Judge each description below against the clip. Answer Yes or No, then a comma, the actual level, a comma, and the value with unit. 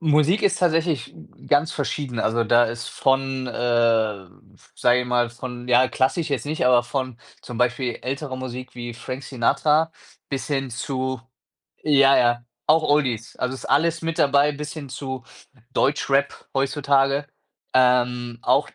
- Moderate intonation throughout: Yes, average, 3.0 semitones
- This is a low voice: Yes, low, 130 Hz